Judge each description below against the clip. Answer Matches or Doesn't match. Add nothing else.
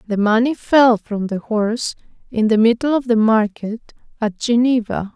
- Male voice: Doesn't match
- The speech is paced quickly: Doesn't match